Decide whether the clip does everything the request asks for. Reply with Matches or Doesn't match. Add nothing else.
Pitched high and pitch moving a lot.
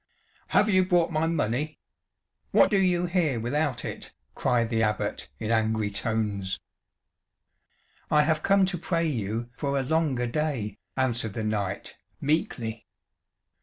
Doesn't match